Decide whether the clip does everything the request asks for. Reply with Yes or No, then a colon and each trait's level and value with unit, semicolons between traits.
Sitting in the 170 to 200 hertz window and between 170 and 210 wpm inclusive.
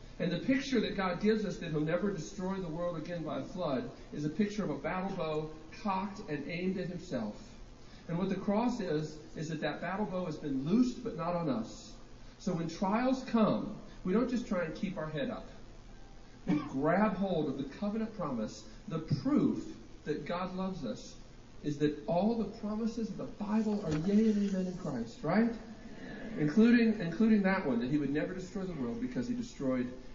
Yes: high, 190 Hz; average, 200 wpm